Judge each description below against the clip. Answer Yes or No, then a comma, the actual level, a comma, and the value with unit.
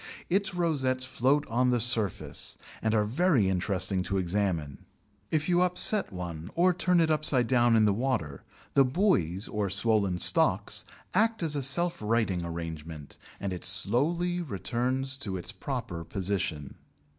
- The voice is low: Yes, low, 115 Hz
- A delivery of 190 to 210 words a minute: No, average, 150 wpm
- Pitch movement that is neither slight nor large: No, wide, 7.7 semitones